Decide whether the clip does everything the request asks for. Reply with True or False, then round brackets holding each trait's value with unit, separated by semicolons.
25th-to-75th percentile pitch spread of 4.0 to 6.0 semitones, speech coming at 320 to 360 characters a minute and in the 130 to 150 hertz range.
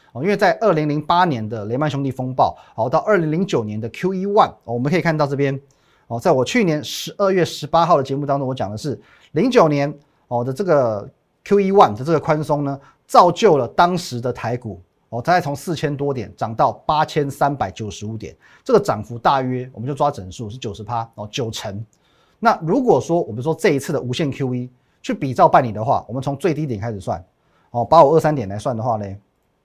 True (5.3 semitones; 325 characters per minute; 140 Hz)